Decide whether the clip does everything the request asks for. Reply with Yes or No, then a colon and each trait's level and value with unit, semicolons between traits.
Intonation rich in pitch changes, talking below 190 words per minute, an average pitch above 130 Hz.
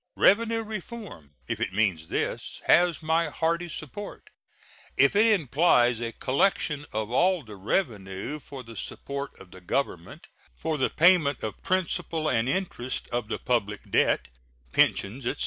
Yes: wide, 7.5 semitones; average, 145 wpm; medium, 140 Hz